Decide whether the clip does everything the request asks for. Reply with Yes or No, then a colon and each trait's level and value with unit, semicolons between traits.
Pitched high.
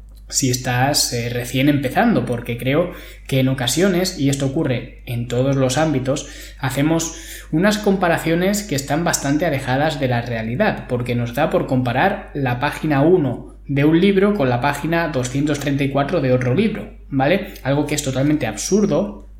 No: medium, 140 Hz